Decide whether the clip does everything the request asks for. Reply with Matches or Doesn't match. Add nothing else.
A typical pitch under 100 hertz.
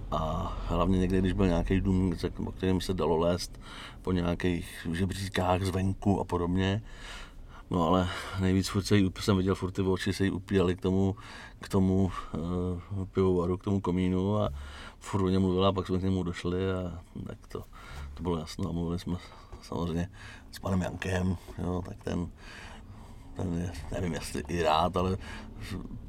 Matches